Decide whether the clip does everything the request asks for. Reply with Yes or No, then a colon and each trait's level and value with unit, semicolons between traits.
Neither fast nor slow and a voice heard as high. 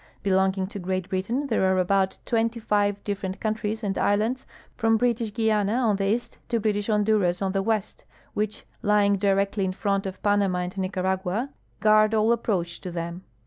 Yes: average, 175 wpm; high, 205 Hz